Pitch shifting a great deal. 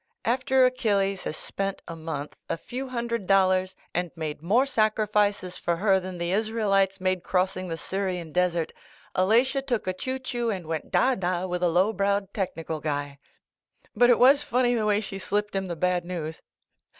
No: average, 3.8 semitones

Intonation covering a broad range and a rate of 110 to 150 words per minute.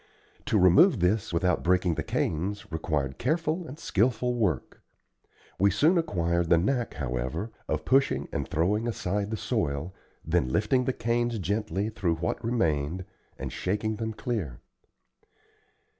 Yes: wide, 5.7 semitones; average, 140 wpm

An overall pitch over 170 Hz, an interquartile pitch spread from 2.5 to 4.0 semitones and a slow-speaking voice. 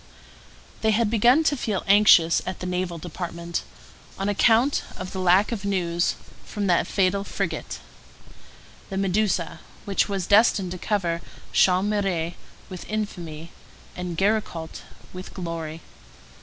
Yes: medium, 185 Hz; average, 3.1 semitones; slow, 130 wpm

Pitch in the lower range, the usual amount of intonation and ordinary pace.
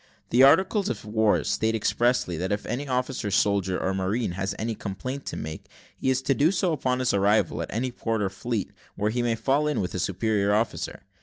No: low, 110 Hz; average, 4.4 semitones; fast, 215 wpm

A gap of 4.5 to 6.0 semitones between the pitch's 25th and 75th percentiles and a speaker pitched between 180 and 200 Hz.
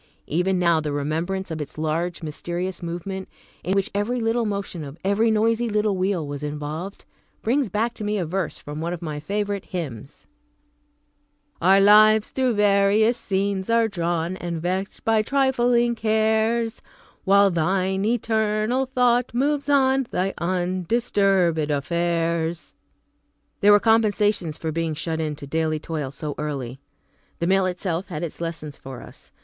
Yes: average, 4.8 semitones; high, 190 Hz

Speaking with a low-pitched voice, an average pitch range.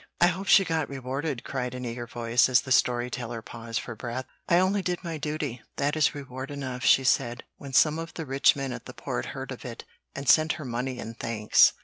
Yes: low, 130 Hz; average, 4.1 semitones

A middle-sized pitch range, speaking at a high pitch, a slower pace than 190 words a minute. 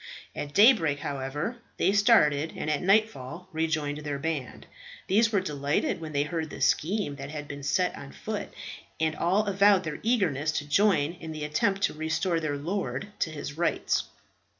No: average, 5.0 semitones; medium, 160 Hz; average, 175 wpm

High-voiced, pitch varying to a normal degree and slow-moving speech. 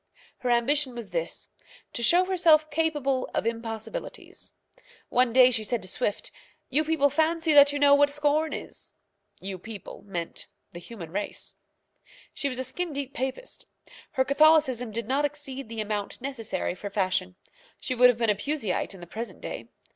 No: very high, 255 Hz; average, 5.0 semitones; average, 170 wpm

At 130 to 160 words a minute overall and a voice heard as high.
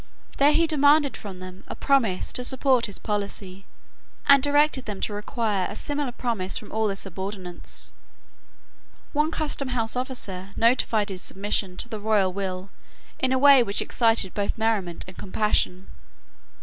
Yes: average, 150 wpm; high, 215 Hz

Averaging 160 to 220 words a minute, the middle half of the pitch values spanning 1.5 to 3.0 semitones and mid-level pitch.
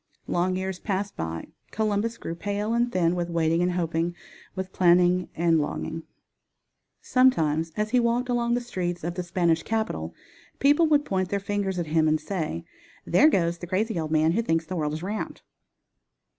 No: average, 180 wpm; average, 4.4 semitones; medium, 180 Hz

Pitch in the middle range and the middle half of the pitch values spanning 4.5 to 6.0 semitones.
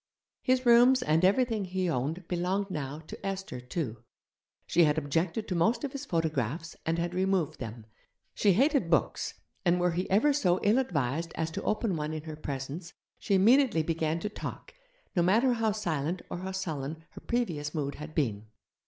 Yes: medium, 175 Hz; average, 4.8 semitones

